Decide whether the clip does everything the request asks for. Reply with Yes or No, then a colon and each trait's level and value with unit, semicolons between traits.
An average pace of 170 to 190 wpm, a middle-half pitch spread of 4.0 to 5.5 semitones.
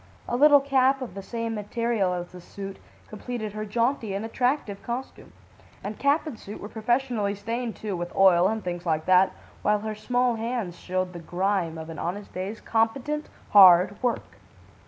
Yes: average, 175 wpm; average, 4.5 semitones